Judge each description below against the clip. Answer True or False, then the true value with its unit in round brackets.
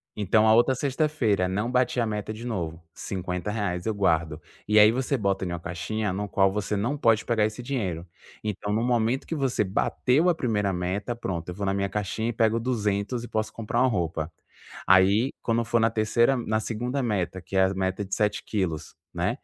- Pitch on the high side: False (105 Hz)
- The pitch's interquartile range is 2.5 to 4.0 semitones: True (3.7 semitones)